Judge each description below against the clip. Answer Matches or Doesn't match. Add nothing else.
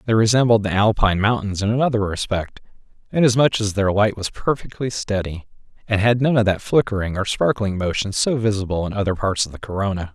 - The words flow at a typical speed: Matches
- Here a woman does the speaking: Doesn't match